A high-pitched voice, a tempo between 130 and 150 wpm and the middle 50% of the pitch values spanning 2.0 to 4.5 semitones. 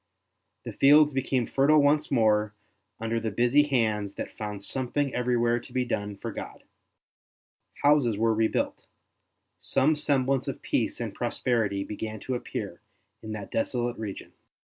No: low, 120 Hz; average, 140 wpm; average, 3.9 semitones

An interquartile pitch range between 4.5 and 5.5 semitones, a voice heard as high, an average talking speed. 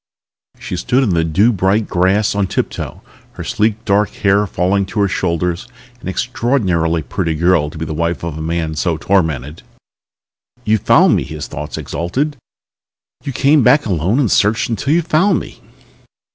No: average, 5.0 semitones; very low, 95 Hz; average, 170 wpm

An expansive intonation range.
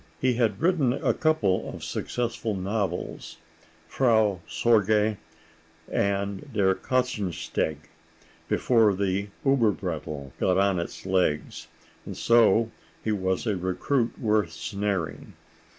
No: average, 3.7 semitones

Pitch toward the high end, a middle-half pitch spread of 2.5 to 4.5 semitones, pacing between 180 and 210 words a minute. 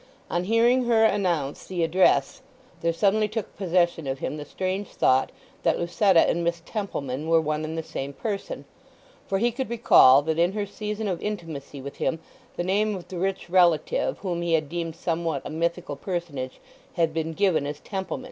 No: medium, 175 Hz; average, 4.0 semitones; average, 185 wpm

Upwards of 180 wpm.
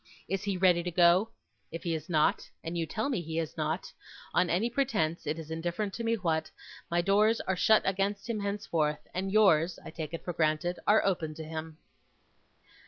Yes: average, 200 wpm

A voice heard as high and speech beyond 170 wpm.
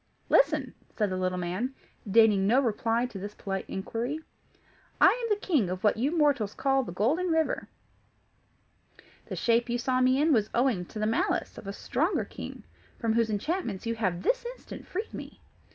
Yes: high, 230 Hz; average, 185 wpm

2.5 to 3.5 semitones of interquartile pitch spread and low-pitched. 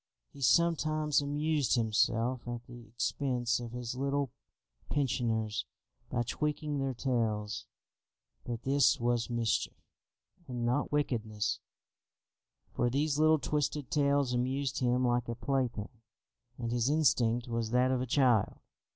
Yes: average, 3.2 semitones; low, 125 Hz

